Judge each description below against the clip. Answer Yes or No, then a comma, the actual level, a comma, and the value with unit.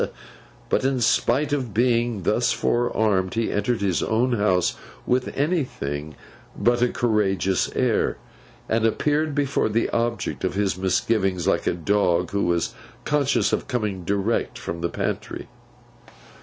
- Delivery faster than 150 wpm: No, average, 140 wpm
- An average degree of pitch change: Yes, average, 4.4 semitones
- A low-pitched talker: Yes, low, 110 Hz